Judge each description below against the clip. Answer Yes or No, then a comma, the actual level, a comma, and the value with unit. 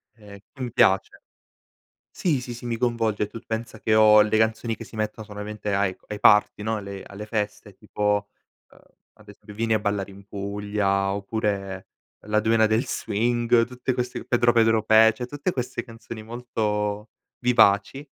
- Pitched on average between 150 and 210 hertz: No, low, 110 Hz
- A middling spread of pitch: No, narrow, 2.2 semitones